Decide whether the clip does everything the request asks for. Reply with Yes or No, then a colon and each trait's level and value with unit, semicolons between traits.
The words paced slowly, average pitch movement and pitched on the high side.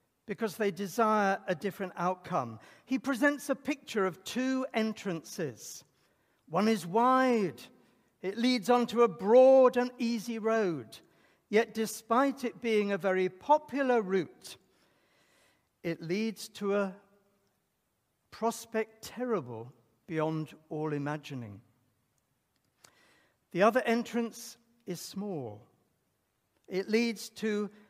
Yes: slow, 105 wpm; average, 4.5 semitones; high, 210 Hz